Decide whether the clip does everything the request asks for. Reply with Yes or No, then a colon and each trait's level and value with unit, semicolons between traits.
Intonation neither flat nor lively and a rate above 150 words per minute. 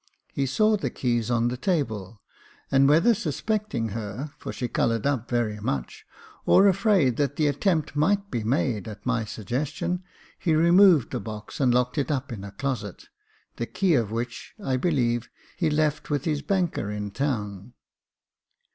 No: wide, 5.7 semitones; average, 165 wpm